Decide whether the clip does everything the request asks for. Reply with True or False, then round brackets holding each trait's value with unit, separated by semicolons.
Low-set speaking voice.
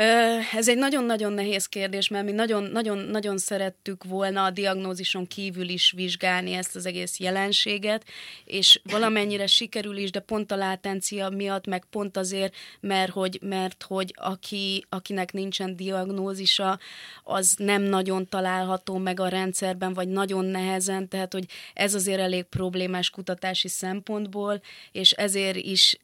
False (195 Hz)